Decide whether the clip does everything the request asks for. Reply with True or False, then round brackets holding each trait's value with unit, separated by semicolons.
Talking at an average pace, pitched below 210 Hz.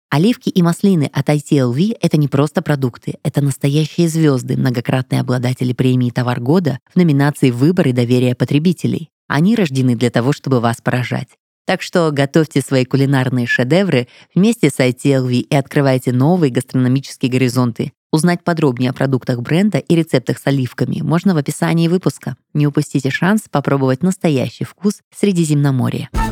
True (145 wpm; 140 Hz)